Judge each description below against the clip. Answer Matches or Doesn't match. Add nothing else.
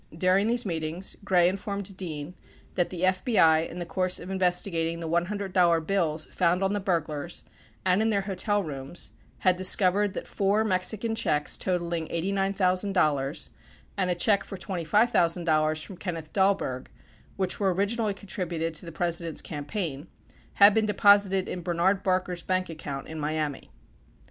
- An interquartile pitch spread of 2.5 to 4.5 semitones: Matches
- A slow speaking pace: Doesn't match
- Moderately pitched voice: Matches